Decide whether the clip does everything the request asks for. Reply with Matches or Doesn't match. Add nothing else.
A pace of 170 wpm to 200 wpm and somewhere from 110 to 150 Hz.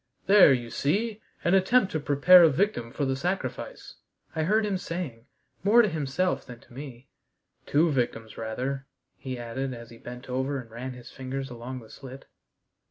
Matches